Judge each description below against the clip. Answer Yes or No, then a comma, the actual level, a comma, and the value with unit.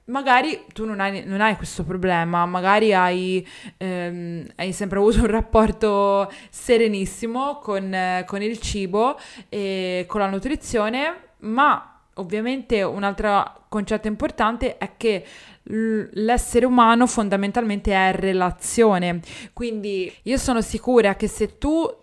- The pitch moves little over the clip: No, average, 3.2 semitones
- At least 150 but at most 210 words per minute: No, average, 125 wpm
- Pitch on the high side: Yes, high, 215 Hz